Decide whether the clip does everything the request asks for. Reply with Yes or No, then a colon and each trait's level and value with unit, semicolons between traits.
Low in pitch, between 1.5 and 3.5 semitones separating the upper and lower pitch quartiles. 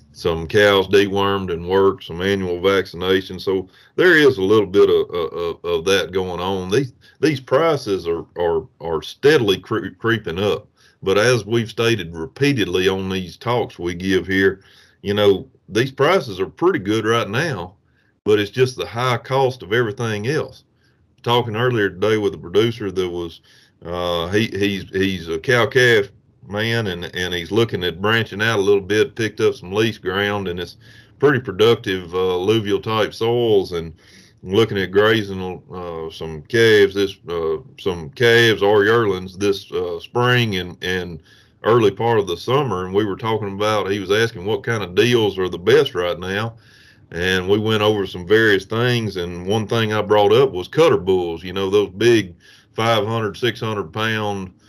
No: low, 105 Hz; average, 3.9 semitones